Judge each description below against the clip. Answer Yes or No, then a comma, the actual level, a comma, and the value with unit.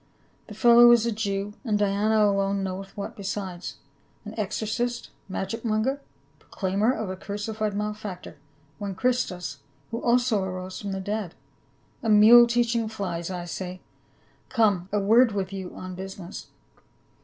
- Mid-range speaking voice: No, high, 205 Hz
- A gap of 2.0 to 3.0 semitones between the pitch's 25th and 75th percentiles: Yes, average, 2.7 semitones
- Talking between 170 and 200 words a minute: No, average, 150 wpm